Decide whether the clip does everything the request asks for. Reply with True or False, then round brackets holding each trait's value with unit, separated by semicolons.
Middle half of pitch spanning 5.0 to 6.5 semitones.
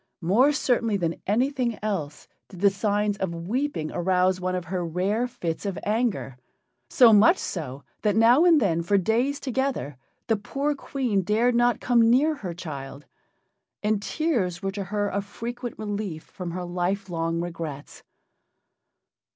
True (5.4 semitones)